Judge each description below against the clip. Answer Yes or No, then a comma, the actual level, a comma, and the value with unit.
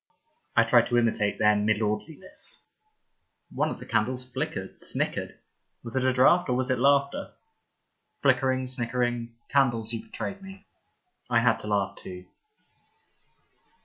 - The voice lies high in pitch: No, low, 120 Hz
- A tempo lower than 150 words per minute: Yes, average, 140 wpm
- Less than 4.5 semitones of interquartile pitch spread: Yes, narrow, 2.5 semitones